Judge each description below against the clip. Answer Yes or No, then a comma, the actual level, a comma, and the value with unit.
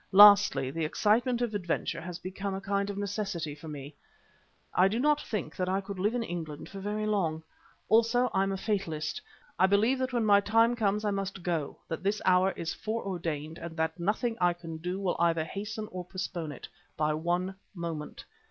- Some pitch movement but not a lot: Yes, average, 4.0 semitones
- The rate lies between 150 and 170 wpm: No, average, 195 wpm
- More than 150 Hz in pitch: Yes, high, 190 Hz